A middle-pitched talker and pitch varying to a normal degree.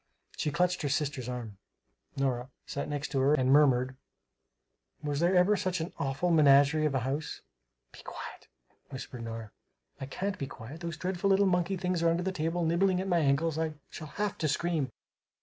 Yes: medium, 155 Hz; average, 4.4 semitones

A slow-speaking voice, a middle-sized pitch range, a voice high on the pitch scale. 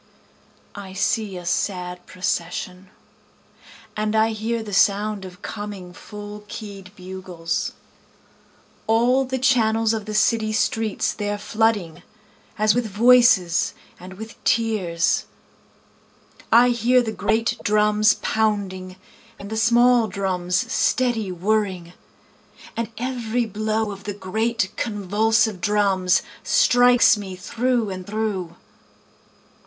Yes: slow, 110 wpm; average, 3.1 semitones; high, 210 Hz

